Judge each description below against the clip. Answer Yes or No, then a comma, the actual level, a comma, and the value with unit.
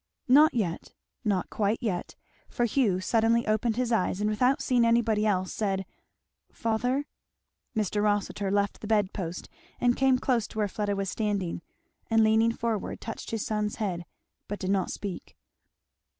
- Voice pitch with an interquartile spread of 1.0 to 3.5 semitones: Yes, narrow, 2.6 semitones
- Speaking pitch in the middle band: No, high, 215 Hz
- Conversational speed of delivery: Yes, average, 165 wpm